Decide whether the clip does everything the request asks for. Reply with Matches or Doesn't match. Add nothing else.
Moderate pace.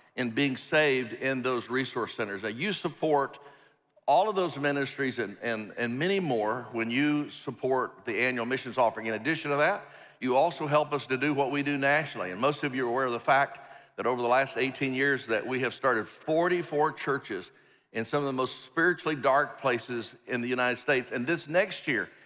Doesn't match